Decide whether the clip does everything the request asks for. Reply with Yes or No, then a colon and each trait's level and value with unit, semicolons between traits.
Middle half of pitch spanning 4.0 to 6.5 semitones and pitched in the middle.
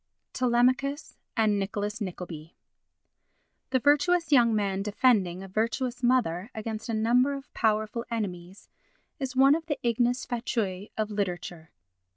No: average, 4.3 semitones; high, 225 Hz